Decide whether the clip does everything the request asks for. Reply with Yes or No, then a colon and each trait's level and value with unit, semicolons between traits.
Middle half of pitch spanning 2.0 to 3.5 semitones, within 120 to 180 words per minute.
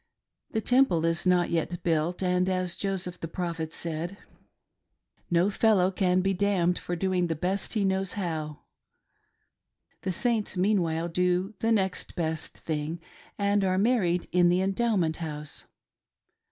Yes: narrow, 2.4 semitones; average, 145 wpm